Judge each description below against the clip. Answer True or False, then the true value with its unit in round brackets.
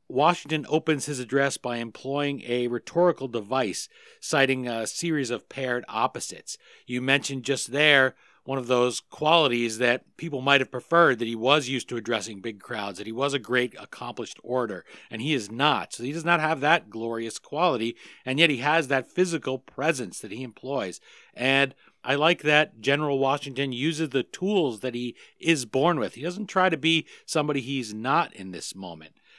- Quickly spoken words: False (185 wpm)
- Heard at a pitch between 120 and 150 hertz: True (135 Hz)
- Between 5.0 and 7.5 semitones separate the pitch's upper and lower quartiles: False (4.0 semitones)